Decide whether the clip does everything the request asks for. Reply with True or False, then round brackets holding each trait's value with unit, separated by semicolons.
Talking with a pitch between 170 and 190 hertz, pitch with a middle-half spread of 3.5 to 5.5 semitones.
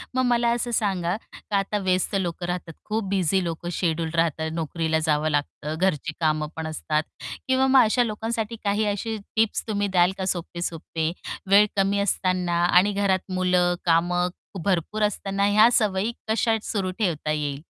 True (185 Hz; 3.9 semitones)